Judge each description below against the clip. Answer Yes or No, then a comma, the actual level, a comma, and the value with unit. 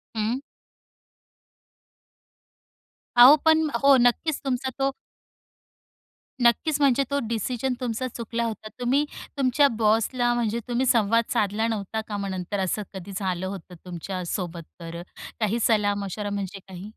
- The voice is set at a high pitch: Yes, high, 225 Hz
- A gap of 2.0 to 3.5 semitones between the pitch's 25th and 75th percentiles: No, average, 3.9 semitones